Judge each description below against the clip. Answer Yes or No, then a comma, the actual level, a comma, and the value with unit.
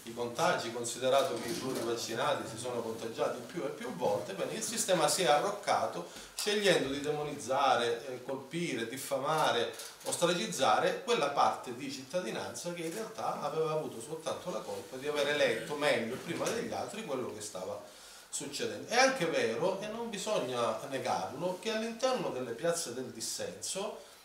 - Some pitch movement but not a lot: No, wide, 7.2 semitones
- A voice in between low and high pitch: Yes, medium, 145 Hz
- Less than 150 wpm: No, average, 155 wpm